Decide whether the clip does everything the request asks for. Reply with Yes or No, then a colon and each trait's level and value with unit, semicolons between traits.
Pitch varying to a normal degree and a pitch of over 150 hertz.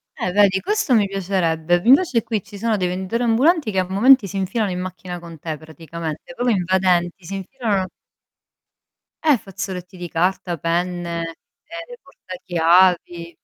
Yes: average, 3.7 semitones; medium, 185 Hz